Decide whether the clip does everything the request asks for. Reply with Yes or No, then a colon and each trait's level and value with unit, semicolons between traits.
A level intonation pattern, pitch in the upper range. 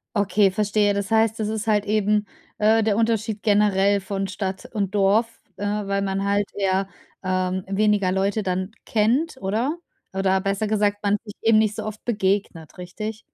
Yes: narrow, 1.8 semitones; high, 205 Hz